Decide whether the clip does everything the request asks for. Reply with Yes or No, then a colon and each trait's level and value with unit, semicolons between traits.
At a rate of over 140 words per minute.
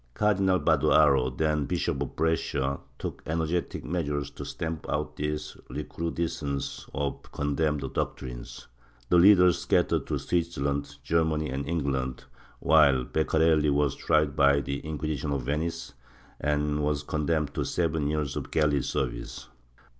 No: slow, 135 wpm